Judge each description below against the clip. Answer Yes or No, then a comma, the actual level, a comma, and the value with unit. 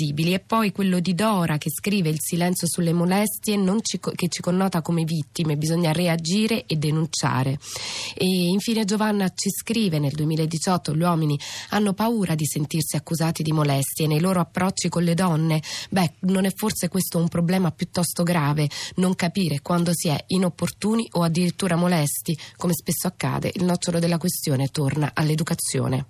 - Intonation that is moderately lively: Yes, average, 3.0 semitones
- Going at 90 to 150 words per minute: No, average, 165 wpm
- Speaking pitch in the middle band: Yes, medium, 170 Hz